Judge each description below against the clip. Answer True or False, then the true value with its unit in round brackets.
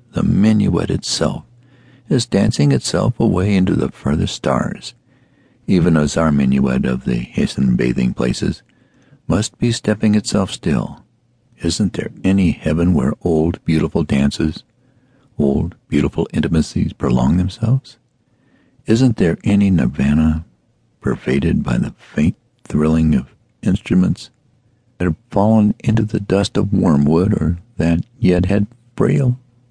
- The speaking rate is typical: False (125 wpm)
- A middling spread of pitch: False (7.0 semitones)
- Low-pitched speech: True (100 Hz)